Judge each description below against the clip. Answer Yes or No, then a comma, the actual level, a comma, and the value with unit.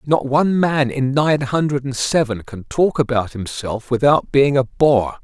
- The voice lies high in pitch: No, low, 135 Hz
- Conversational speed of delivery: Yes, average, 185 wpm